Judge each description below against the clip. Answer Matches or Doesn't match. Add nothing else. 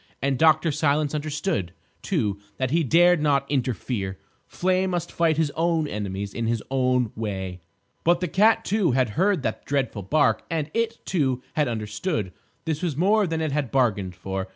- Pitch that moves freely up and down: Matches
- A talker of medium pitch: Matches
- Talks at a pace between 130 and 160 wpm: Doesn't match